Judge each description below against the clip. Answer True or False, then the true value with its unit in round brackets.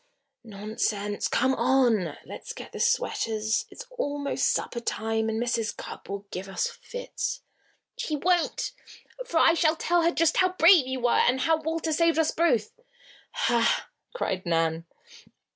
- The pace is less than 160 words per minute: True (150 wpm)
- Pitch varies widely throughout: True (7.2 semitones)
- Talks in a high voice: True (260 Hz)